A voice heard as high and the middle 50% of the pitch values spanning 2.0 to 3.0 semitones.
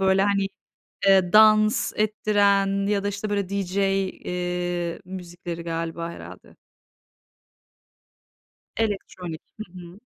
Yes: high, 195 Hz; narrow, 2.4 semitones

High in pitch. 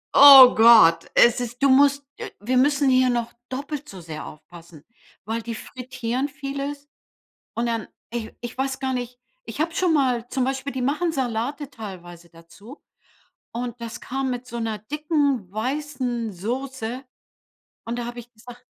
Yes: very high, 250 Hz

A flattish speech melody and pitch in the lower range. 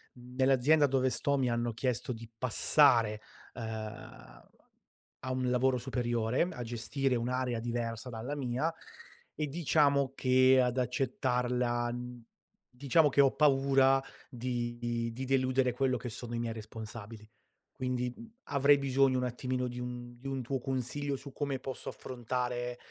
Yes: narrow, 2.0 semitones; low, 125 Hz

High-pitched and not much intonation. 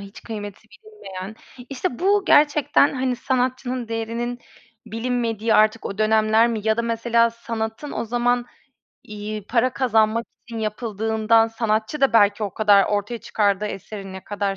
Yes: high, 225 Hz; narrow, 2.2 semitones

